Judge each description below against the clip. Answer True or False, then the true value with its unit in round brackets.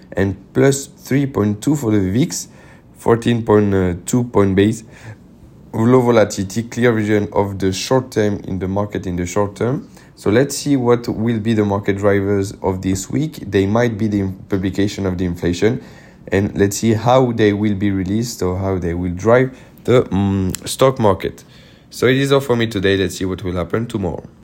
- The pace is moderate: True (180 wpm)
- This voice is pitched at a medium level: False (105 Hz)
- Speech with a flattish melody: False (3.5 semitones)